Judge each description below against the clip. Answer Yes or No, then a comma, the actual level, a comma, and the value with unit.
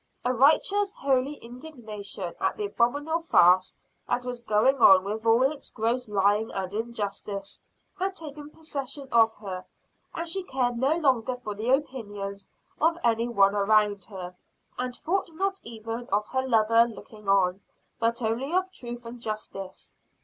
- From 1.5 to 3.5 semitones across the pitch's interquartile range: No, average, 4.6 semitones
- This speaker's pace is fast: No, average, 155 wpm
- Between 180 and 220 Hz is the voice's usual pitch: No, high, 235 Hz